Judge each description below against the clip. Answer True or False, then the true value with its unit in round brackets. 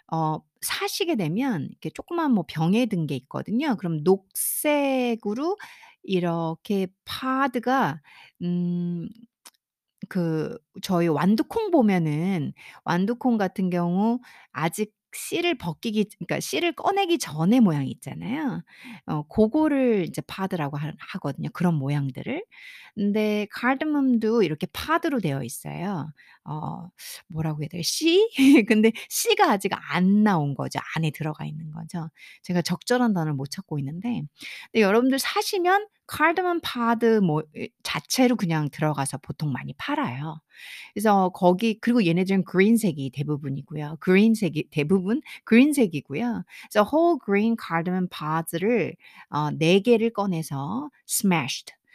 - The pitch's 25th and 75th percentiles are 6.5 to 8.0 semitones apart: True (7.1 semitones)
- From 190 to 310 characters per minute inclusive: True (290 characters per minute)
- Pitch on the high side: True (195 Hz)